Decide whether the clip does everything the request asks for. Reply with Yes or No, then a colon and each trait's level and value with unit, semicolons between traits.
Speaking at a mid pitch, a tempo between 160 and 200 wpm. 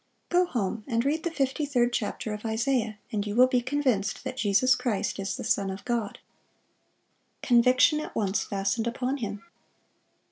No: high, 235 Hz; average, 170 wpm